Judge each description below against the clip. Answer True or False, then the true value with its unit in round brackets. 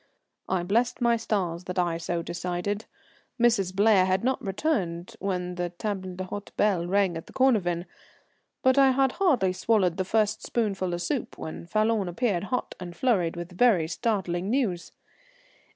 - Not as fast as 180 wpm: True (160 wpm)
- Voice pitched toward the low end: False (190 Hz)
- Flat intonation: False (4.4 semitones)